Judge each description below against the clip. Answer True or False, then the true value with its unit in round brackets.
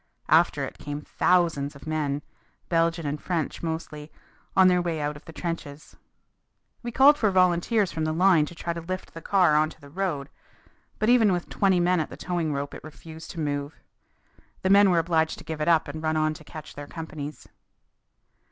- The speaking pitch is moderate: True (160 Hz)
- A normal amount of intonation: True (3.0 semitones)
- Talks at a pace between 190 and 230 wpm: True (200 wpm)